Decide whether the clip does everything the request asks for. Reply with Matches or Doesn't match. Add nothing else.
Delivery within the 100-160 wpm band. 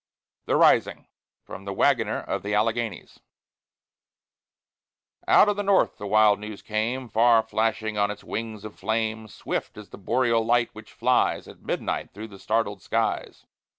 Matches